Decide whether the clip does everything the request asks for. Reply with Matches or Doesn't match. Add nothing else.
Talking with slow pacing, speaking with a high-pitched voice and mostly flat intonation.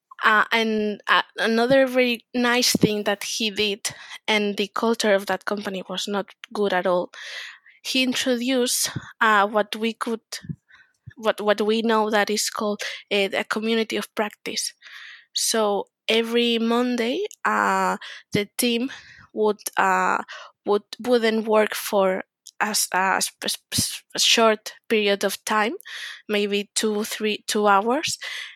Matches